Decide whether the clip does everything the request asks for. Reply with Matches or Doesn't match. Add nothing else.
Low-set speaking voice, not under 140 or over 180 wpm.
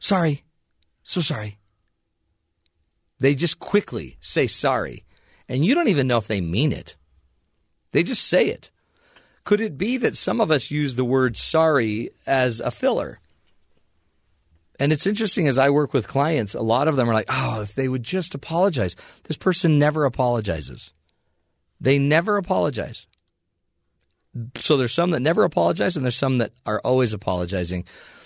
Matches